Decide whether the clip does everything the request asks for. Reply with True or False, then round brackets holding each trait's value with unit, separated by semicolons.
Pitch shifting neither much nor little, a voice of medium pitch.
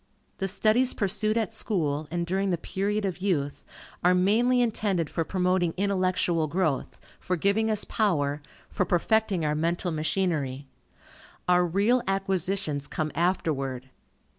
True (3.9 semitones; 180 Hz)